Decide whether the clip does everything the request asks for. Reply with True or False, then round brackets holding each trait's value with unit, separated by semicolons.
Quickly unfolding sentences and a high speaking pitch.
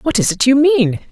True (270 wpm; 250 Hz)